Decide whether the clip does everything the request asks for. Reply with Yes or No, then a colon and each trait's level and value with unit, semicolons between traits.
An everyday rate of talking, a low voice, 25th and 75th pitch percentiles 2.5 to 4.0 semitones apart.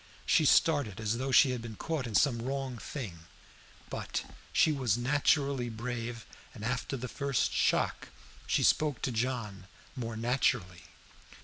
Yes: average, 145 wpm; low, 125 Hz; average, 3.3 semitones